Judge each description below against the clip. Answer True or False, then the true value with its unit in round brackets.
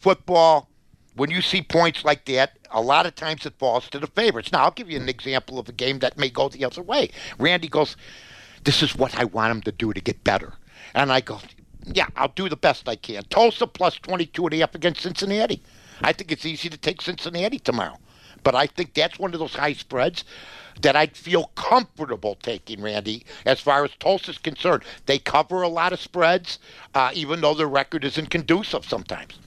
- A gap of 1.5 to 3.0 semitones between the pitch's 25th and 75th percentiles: False (4.7 semitones)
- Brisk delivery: True (215 wpm)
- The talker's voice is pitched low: False (155 Hz)